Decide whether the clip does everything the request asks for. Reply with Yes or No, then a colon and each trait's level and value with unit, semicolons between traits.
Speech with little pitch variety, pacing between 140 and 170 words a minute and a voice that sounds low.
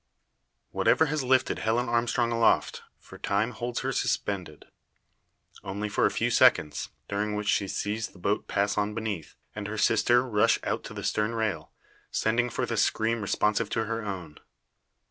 Yes: narrow, 2.3 semitones; average, 165 wpm; low, 110 Hz